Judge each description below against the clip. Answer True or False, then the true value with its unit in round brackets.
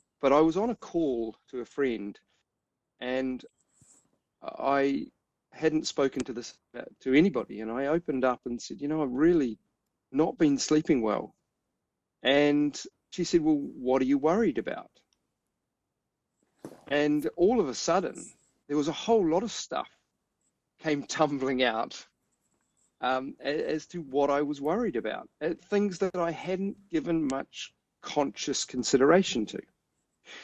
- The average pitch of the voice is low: False (150 Hz)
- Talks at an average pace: True (145 wpm)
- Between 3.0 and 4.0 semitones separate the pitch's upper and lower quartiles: False (5.1 semitones)